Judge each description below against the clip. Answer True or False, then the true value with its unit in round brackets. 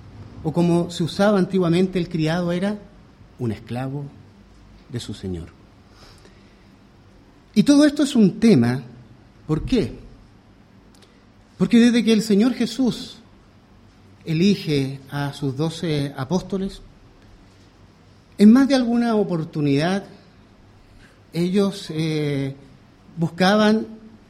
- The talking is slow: True (100 wpm)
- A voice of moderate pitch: True (145 Hz)